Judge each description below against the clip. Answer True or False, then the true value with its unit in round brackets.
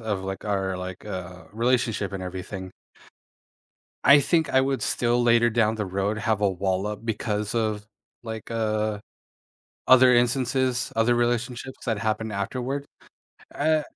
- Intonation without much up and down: False (3.3 semitones)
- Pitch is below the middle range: True (110 Hz)